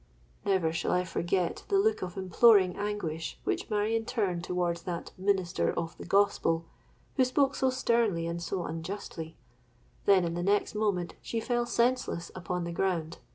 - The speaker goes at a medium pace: Yes, average, 160 wpm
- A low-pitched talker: No, medium, 185 Hz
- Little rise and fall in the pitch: No, average, 4.1 semitones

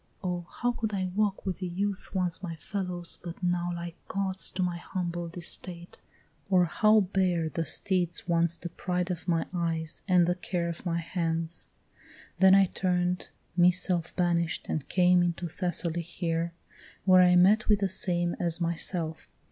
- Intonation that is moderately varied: No, narrow, 1.6 semitones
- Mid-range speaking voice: Yes, medium, 175 Hz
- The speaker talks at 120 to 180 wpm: Yes, average, 170 wpm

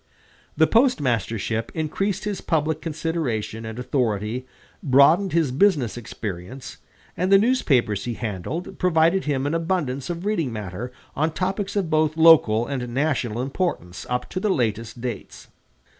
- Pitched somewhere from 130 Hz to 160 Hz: Yes, medium, 140 Hz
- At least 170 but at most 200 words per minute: No, average, 140 wpm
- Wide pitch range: Yes, wide, 6.3 semitones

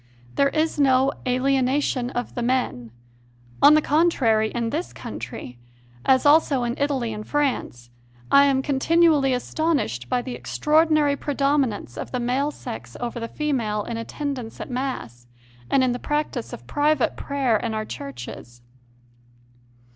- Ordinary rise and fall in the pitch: Yes, average, 4.1 semitones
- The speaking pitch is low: No, very high, 260 Hz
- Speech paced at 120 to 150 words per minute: Yes, average, 145 wpm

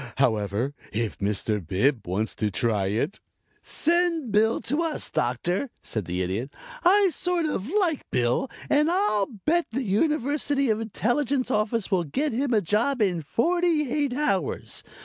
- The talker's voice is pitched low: No, high, 220 Hz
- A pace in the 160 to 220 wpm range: No, average, 150 wpm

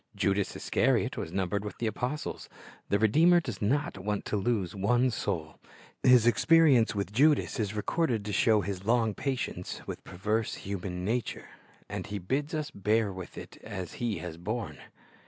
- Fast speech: No, average, 165 wpm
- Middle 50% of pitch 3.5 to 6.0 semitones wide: Yes, average, 3.9 semitones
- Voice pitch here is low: Yes, low, 105 Hz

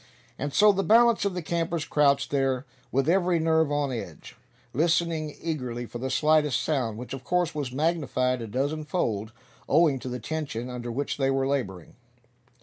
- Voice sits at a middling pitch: Yes, medium, 145 Hz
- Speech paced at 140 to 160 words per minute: No, average, 175 wpm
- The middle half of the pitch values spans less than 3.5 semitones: No, average, 4.3 semitones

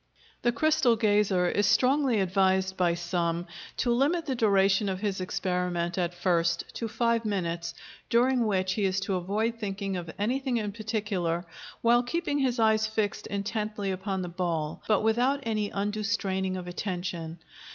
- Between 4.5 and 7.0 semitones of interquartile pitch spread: No, average, 3.8 semitones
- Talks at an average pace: Yes, average, 160 wpm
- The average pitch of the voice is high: Yes, high, 200 Hz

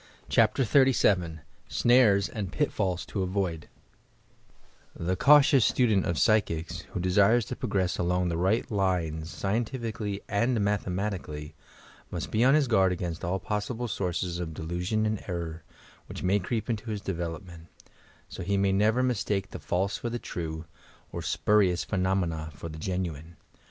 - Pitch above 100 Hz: No, very low, 95 Hz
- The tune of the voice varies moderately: Yes, average, 3.8 semitones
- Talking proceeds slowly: No, average, 155 wpm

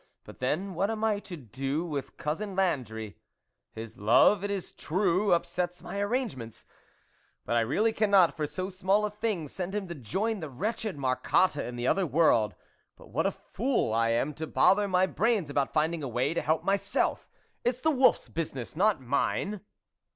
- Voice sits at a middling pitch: Yes, medium, 175 Hz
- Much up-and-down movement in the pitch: Yes, wide, 6.8 semitones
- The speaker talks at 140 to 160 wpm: No, average, 190 wpm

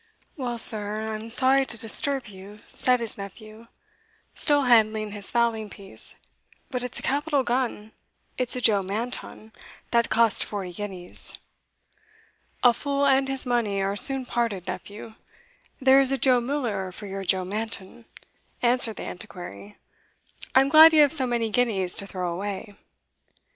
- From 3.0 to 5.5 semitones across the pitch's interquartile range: Yes, average, 4.0 semitones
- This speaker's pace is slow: No, average, 160 wpm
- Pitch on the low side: No, high, 225 Hz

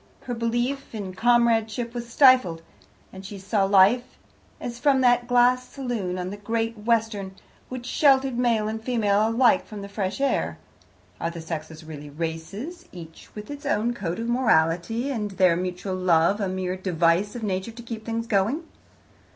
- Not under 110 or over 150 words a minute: No, average, 165 wpm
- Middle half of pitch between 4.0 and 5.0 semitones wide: Yes, average, 4.5 semitones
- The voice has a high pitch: Yes, high, 215 Hz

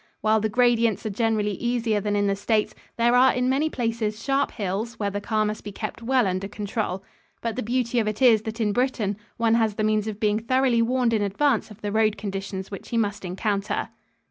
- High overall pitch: Yes, high, 220 Hz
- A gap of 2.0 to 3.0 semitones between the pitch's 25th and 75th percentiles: Yes, narrow, 2.4 semitones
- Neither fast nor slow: No, fast, 220 wpm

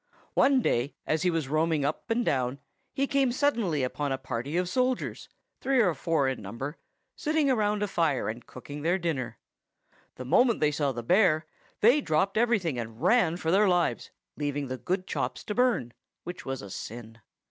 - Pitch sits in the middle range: Yes, medium, 160 Hz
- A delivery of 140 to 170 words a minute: No, average, 185 wpm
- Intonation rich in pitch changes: Yes, wide, 8.1 semitones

